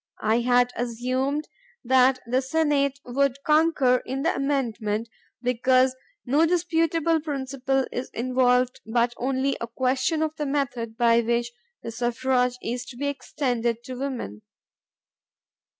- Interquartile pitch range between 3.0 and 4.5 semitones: No, narrow, 2.6 semitones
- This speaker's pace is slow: Yes, slow, 130 wpm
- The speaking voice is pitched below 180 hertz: No, very high, 255 Hz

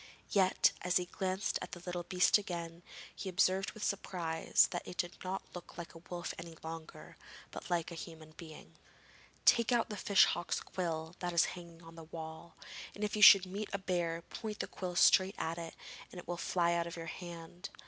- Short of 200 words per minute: No, fast, 205 wpm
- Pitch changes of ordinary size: No, narrow, 2.1 semitones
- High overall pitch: No, medium, 175 Hz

